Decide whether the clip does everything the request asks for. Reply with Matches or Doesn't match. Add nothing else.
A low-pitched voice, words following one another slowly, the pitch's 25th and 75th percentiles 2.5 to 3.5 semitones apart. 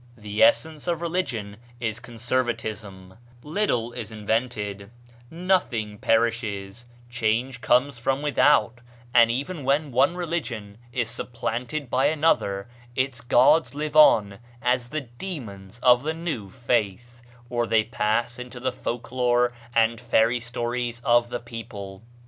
Matches